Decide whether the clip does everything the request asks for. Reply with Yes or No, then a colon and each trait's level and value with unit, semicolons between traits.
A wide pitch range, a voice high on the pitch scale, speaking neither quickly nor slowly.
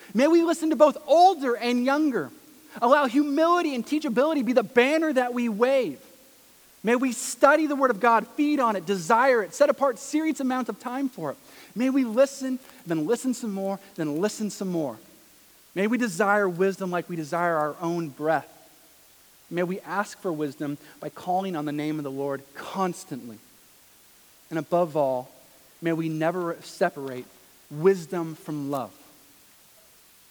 Yes: wide, 8.0 semitones; high, 210 Hz; average, 165 wpm